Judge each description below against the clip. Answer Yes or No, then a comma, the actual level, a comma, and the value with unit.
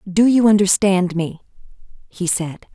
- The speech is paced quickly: No, slow, 130 wpm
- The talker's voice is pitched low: No, high, 190 Hz